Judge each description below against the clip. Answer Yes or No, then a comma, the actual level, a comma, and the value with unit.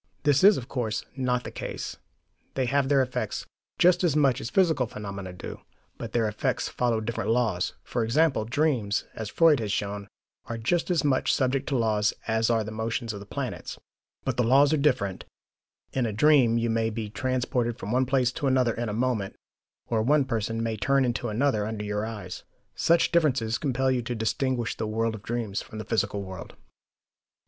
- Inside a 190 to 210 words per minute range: Yes, average, 195 wpm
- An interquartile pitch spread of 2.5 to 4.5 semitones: Yes, average, 3.4 semitones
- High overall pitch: No, low, 120 Hz